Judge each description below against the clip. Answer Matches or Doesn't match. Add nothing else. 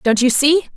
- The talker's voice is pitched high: Matches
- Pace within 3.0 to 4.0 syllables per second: Doesn't match